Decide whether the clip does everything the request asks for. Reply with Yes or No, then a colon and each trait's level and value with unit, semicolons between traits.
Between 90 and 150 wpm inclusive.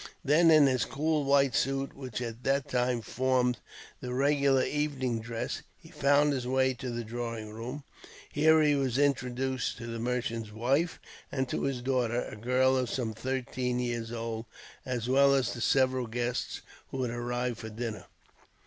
No: average, 170 wpm